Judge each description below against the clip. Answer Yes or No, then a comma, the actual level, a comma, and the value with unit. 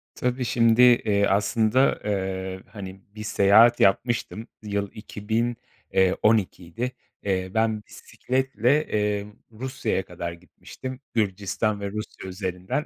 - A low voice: Yes, low, 105 Hz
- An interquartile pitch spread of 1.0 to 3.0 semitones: No, average, 3.6 semitones